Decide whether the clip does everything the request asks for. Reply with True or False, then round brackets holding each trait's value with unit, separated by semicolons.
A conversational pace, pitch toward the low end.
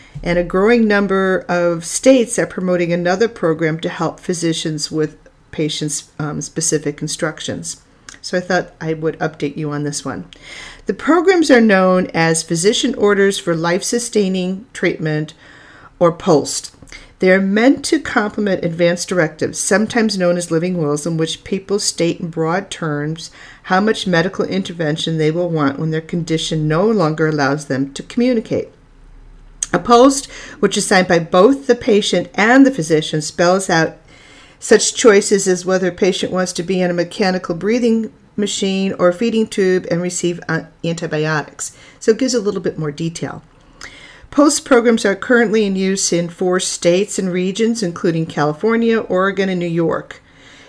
False (160 wpm; 180 Hz)